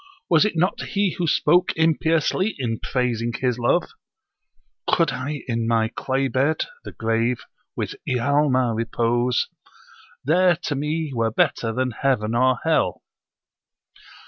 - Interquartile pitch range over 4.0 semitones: Yes, average, 5.1 semitones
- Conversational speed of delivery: No, slow, 130 wpm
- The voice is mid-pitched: No, low, 130 Hz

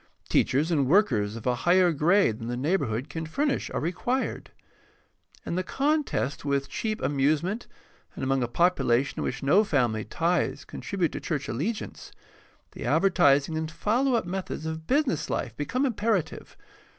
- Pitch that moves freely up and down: Yes, wide, 6.5 semitones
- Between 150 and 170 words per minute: Yes, average, 155 wpm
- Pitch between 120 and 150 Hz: No, medium, 160 Hz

